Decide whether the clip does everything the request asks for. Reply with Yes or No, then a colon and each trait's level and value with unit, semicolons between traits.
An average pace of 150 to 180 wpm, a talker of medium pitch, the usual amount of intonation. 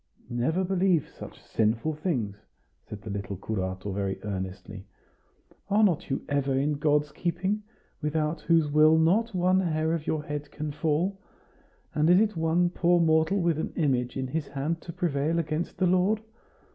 Yes: average, 160 wpm; medium, 155 Hz; average, 4.4 semitones